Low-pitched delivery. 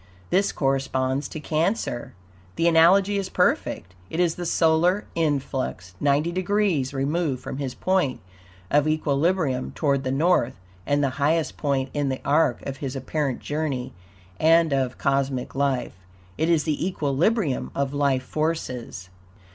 No: medium, 145 Hz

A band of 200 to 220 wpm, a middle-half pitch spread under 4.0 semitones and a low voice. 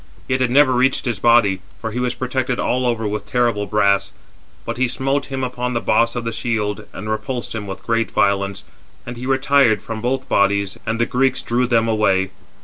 Yes: fast, 205 wpm; average, 3.2 semitones; low, 115 Hz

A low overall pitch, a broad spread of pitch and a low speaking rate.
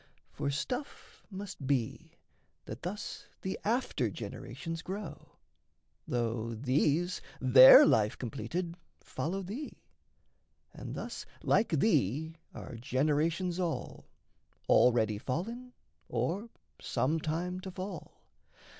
No: medium, 160 Hz; wide, 6.7 semitones; slow, 100 wpm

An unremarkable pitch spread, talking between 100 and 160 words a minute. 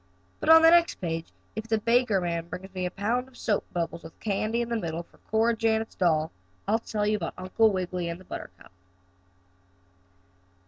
No: average, 4.3 semitones; average, 190 wpm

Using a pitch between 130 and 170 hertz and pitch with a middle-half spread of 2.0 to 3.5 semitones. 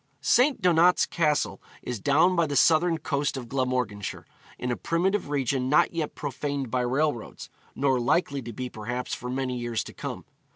No: medium, 140 Hz; average, 4.3 semitones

